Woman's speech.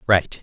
No: male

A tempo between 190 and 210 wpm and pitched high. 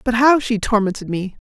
Yes: fast, 205 wpm; high, 220 Hz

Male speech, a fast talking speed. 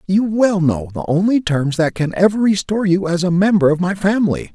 Yes: male; fast, 225 wpm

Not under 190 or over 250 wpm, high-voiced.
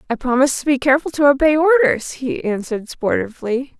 No: average, 175 wpm; very high, 270 Hz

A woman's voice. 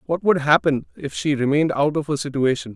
No: male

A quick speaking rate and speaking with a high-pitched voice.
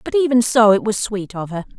Yes: fast, 270 wpm; high, 220 Hz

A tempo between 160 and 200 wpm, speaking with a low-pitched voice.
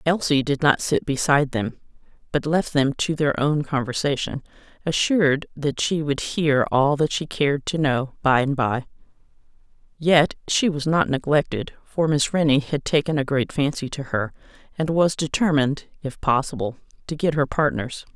No: average, 170 wpm; medium, 145 Hz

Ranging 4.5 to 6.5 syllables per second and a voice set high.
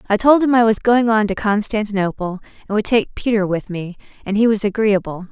Yes: 5.7 syllables/s; high, 210 Hz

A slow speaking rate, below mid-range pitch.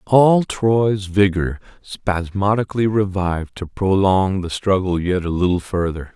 Yes: slow, 125 wpm; very low, 95 Hz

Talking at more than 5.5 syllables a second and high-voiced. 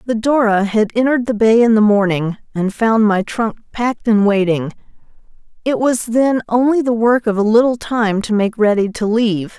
No: 5.0 syllables/s; high, 220 Hz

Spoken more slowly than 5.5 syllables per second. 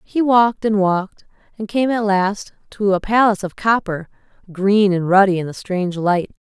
Yes: 5.1 syllables/s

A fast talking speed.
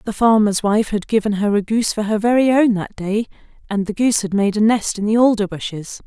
Yes: fast, 245 wpm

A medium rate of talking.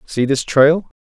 Yes: average, 175 wpm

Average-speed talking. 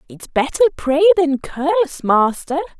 No: slow, 130 wpm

